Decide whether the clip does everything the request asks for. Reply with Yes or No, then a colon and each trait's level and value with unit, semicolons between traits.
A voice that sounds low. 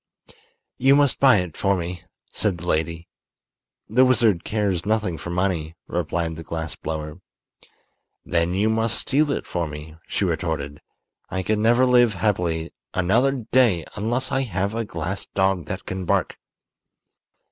Yes: very low, 95 Hz